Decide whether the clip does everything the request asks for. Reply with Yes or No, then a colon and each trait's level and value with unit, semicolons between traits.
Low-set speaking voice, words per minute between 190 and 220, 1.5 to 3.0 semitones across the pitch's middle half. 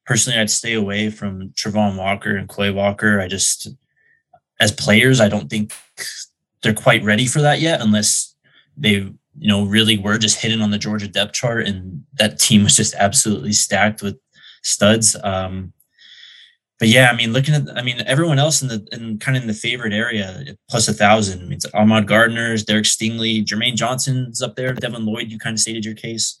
Yes: low, 110 Hz; average, 200 wpm; narrow, 2.5 semitones